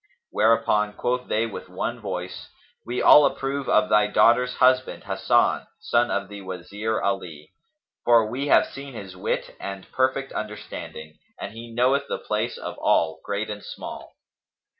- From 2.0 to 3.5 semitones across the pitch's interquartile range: No, average, 4.2 semitones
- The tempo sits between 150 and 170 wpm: Yes, average, 155 wpm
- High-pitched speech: No, low, 110 Hz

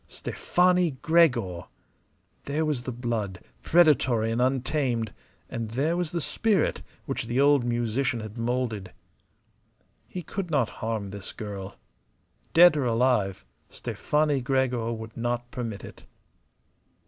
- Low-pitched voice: Yes, low, 125 Hz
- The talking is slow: Yes, slow, 125 wpm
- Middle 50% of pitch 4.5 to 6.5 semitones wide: Yes, average, 4.8 semitones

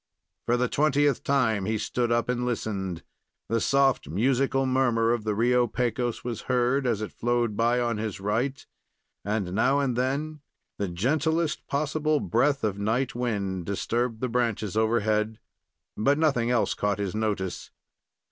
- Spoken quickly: No, average, 155 wpm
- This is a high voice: No, low, 120 Hz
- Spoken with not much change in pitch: No, average, 3.7 semitones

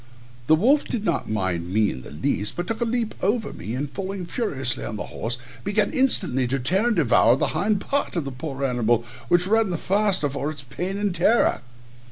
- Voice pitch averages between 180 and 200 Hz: No, medium, 170 Hz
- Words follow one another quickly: Yes, fast, 215 wpm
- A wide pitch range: Yes, wide, 8.7 semitones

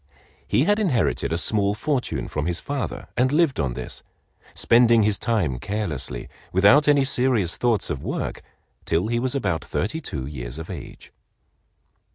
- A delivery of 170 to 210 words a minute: No, average, 160 wpm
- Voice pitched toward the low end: Yes, low, 110 Hz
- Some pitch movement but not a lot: No, wide, 8.0 semitones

